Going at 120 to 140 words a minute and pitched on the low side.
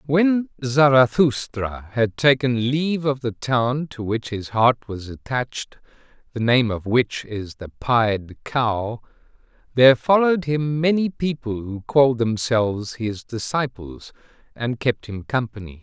Yes: slow, 135 wpm; low, 125 Hz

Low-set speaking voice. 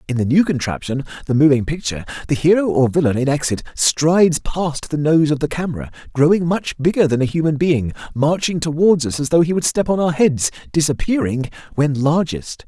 No: medium, 150 Hz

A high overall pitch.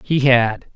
No: low, 130 Hz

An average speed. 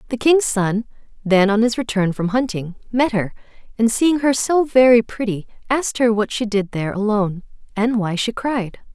Yes: average, 190 wpm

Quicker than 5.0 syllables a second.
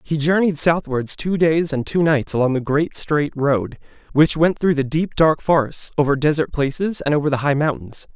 No: 4.9 syllables/s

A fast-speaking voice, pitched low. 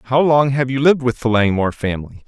Yes: fast, 235 wpm; low, 125 Hz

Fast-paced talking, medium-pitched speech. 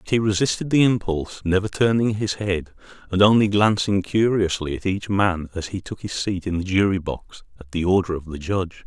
No: fast, 210 wpm; very low, 95 Hz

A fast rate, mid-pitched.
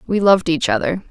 Yes: fast, 215 wpm; medium, 175 Hz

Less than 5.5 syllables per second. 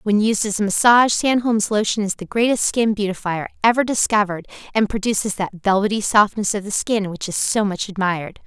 No: 5.7 syllables/s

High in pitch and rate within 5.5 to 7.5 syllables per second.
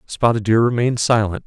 No: low, 115 Hz; 5.9 syllables/s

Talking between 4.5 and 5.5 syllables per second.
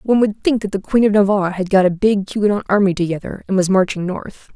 No: 6.4 syllables/s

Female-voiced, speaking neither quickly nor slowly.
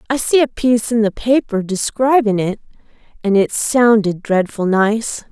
Yes: female; average, 160 wpm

